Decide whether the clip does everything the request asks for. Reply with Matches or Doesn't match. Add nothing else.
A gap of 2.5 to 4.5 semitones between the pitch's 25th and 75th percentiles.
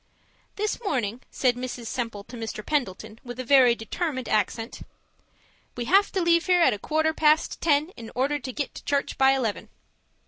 Doesn't match